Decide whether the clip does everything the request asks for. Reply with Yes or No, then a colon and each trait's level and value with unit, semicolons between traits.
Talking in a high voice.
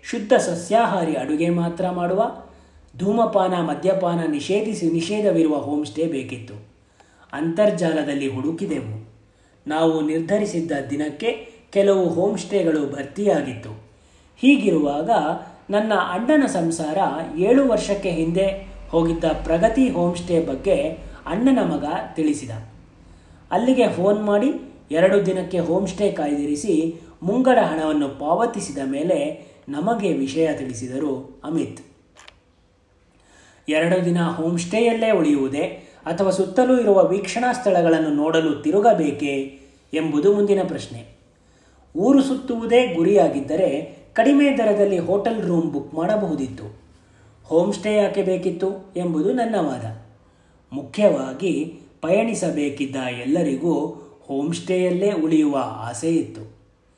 No: medium, 165 Hz